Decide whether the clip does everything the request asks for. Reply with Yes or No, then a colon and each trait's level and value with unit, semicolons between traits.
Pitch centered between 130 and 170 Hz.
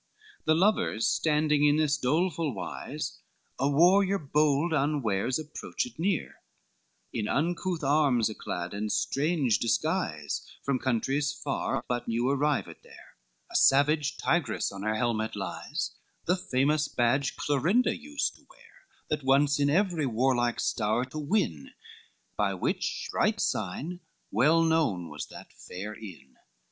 Yes: medium, 140 Hz